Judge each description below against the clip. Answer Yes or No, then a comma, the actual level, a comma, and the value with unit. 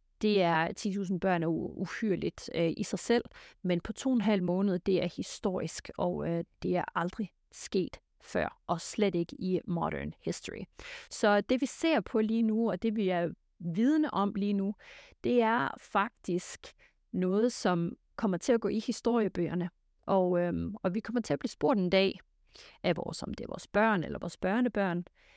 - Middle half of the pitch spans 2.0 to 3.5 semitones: No, average, 4.0 semitones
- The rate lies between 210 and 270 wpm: No, average, 190 wpm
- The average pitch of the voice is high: Yes, high, 200 Hz